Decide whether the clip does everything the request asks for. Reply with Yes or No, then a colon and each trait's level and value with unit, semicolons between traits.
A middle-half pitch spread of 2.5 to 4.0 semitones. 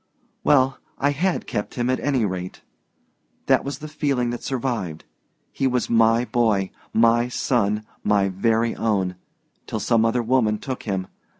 Yes: average, 3.7 semitones